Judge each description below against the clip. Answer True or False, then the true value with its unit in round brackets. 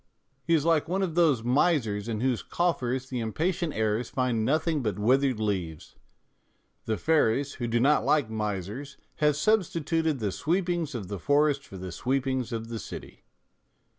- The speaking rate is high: False (165 wpm)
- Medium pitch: False (130 Hz)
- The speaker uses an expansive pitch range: True (5.9 semitones)